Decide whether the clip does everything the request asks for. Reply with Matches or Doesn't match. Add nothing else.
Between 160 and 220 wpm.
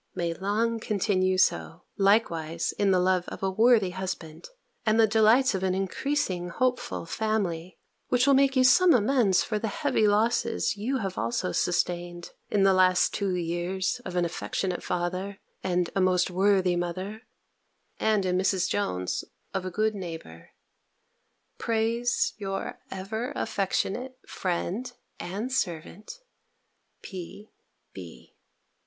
Doesn't match